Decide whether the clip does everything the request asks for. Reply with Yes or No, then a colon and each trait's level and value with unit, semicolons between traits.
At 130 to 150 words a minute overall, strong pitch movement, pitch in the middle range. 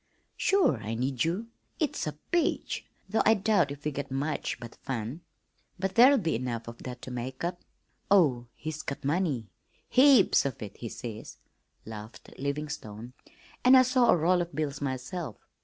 No: average, 170 wpm; wide, 7.3 semitones; medium, 145 Hz